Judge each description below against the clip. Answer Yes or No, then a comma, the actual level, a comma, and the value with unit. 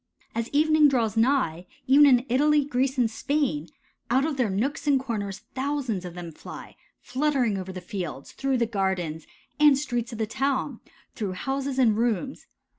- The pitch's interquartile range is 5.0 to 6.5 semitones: Yes, wide, 5.4 semitones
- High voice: Yes, high, 245 Hz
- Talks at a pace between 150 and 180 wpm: Yes, average, 170 wpm